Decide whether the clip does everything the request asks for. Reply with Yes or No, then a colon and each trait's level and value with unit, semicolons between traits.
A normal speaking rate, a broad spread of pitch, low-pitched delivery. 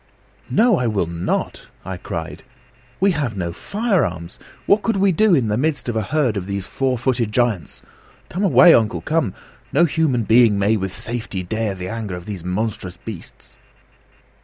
Yes: average, 175 wpm; wide, 7.9 semitones; low, 115 Hz